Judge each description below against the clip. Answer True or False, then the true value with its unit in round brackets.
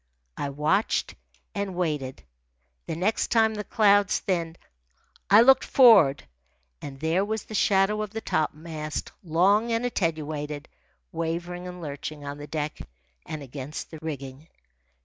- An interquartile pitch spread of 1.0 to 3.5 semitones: False (5.2 semitones)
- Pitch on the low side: False (165 Hz)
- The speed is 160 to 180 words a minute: False (135 wpm)